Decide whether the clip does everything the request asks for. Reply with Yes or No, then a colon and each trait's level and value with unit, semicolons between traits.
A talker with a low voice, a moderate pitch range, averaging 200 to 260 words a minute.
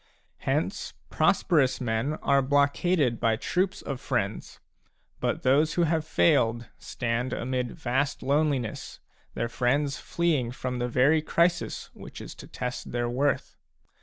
No: low, 130 Hz; average, 3.8 semitones; slow, 135 wpm